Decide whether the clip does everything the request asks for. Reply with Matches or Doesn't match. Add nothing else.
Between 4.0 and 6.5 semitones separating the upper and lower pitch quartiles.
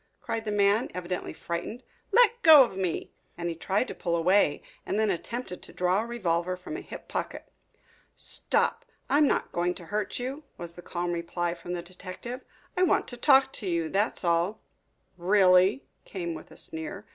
Matches